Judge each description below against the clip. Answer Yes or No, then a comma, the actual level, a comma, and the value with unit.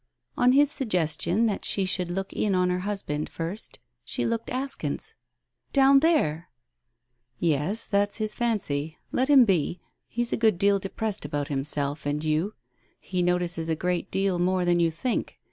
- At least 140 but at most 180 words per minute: Yes, average, 165 wpm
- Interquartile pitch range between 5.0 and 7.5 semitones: Yes, average, 5.3 semitones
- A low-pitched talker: No, medium, 185 Hz